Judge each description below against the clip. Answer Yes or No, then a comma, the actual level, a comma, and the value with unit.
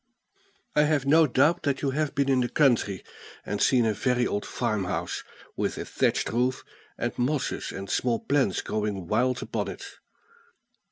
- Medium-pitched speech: No, low, 125 Hz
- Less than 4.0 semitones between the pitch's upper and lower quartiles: No, average, 4.5 semitones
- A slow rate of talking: No, average, 165 wpm